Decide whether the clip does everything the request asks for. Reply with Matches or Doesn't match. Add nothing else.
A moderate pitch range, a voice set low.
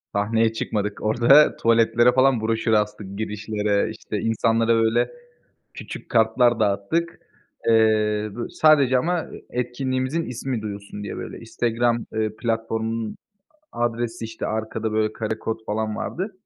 Doesn't match